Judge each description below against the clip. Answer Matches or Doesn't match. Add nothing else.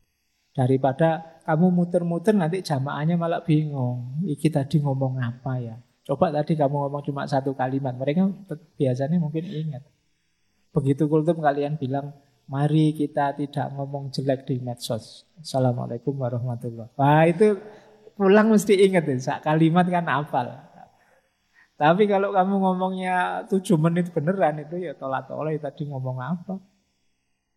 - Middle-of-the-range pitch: Matches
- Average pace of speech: Doesn't match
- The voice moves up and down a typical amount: Matches